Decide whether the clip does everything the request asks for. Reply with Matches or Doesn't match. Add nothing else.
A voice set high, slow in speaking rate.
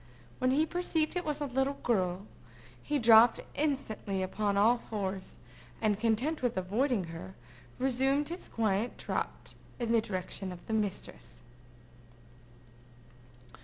Matches